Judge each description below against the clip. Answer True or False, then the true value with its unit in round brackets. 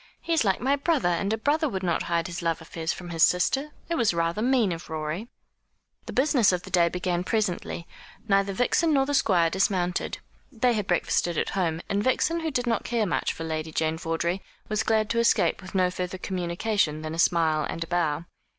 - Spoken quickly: True (215 wpm)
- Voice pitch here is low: False (185 Hz)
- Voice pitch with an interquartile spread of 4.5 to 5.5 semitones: True (5.2 semitones)